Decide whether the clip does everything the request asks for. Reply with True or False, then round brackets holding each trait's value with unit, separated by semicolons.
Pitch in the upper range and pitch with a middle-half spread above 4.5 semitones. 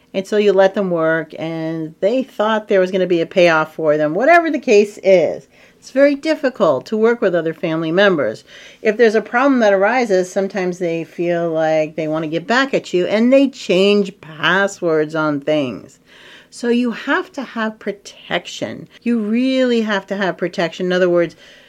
True (195 Hz; 5.4 semitones)